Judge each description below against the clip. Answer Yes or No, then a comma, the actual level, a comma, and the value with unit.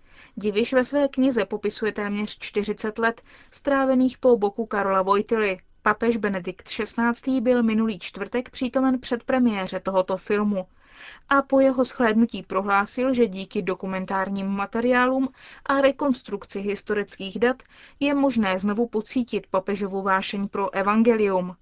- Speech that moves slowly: No, average, 125 wpm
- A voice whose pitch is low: No, high, 215 Hz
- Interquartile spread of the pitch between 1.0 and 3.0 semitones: No, average, 4.0 semitones